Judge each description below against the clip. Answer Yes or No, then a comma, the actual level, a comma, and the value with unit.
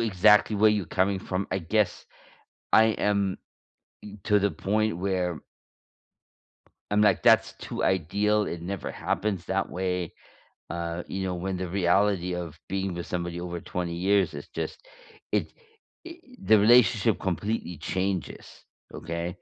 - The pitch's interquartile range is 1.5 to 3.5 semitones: Yes, average, 2.9 semitones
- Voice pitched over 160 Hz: No, very low, 95 Hz